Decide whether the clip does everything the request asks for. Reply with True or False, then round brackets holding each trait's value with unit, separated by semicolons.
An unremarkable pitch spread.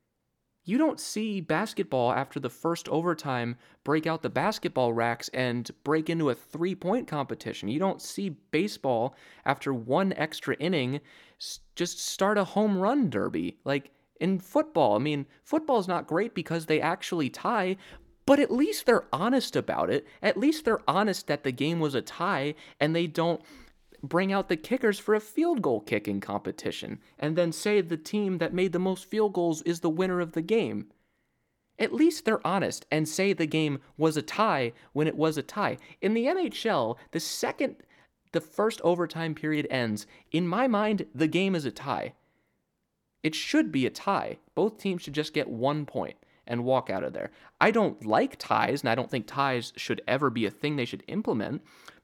False (5.9 semitones)